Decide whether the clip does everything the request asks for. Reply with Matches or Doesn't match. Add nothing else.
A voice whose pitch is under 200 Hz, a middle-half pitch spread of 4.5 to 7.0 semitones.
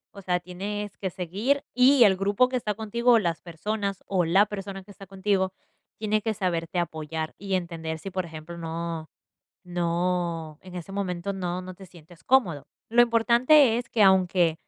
Doesn't match